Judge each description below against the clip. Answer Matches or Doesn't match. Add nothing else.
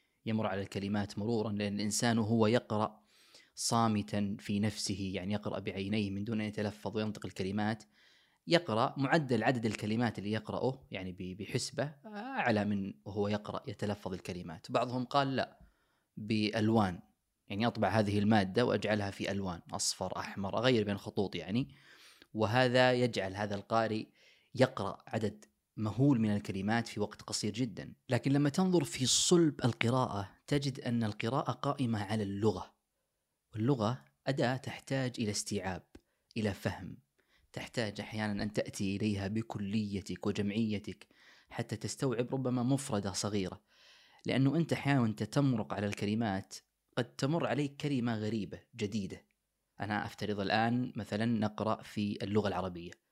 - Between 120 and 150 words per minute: Matches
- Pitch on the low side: Matches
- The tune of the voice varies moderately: Matches